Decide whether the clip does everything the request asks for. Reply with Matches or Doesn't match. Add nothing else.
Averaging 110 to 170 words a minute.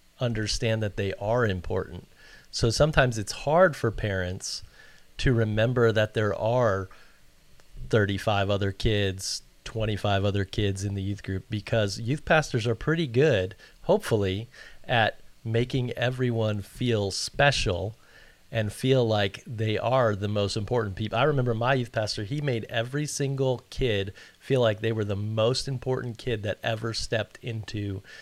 Matches